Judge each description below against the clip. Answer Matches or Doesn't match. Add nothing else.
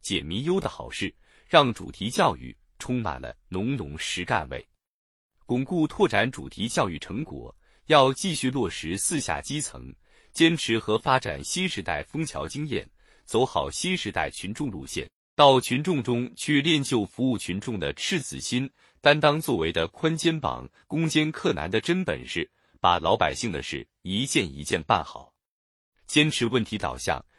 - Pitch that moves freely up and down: Matches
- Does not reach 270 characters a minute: Matches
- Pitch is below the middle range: Matches